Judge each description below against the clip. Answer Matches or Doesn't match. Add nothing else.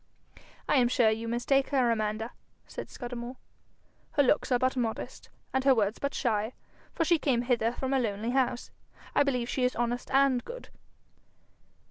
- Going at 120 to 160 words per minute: Doesn't match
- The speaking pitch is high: Matches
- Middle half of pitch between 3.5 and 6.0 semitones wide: Doesn't match